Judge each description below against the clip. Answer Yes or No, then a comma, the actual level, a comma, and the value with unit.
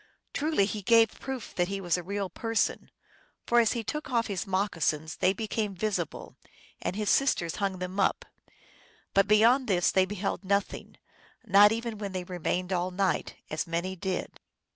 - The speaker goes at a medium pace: Yes, average, 170 wpm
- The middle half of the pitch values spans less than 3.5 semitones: Yes, average, 3.0 semitones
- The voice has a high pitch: Yes, high, 195 Hz